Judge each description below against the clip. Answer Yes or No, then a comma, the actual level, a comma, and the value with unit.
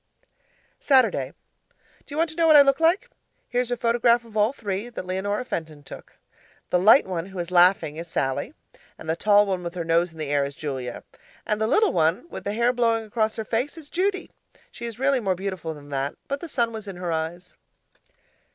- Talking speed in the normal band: No, fast, 215 wpm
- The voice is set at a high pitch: Yes, high, 205 Hz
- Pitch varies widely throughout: Yes, wide, 6.3 semitones